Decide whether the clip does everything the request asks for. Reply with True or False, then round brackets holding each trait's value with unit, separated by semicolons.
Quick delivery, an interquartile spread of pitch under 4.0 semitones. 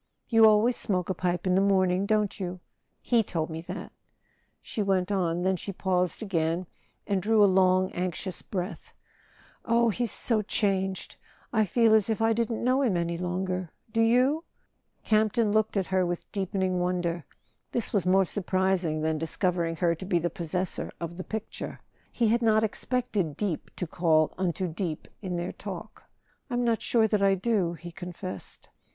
False (170 wpm; 3.5 semitones)